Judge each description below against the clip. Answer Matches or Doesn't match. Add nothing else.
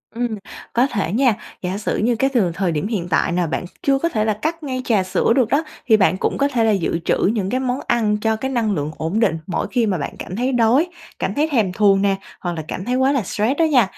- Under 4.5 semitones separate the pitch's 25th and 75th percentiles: Doesn't match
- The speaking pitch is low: Doesn't match